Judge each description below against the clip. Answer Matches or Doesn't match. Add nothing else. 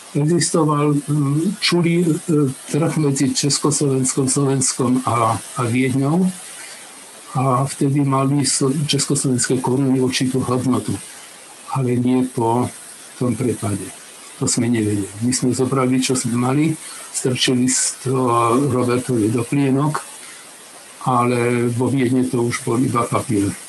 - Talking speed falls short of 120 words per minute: Matches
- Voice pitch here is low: Matches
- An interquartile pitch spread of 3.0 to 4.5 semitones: Doesn't match